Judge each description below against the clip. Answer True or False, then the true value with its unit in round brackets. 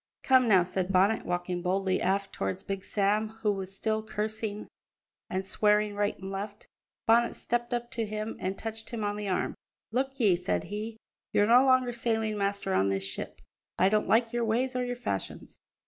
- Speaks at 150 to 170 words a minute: False (190 wpm)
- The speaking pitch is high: True (210 Hz)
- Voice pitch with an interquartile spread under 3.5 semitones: True (3.0 semitones)